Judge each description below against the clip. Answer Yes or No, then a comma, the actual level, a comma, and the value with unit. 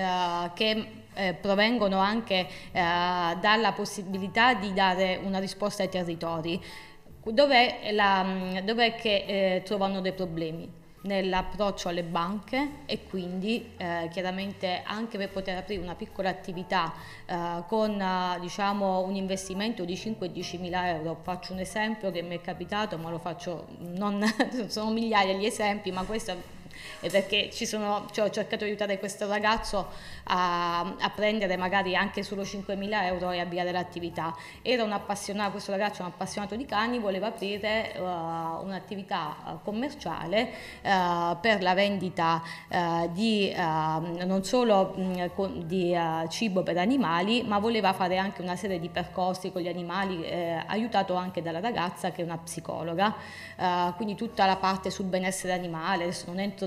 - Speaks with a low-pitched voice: No, high, 190 Hz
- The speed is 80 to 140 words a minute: No, average, 150 wpm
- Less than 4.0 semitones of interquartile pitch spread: Yes, narrow, 2.5 semitones